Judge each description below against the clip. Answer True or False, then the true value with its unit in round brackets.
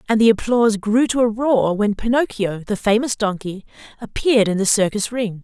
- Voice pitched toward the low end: False (220 Hz)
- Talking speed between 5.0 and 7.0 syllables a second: True (5.4 syllables/s)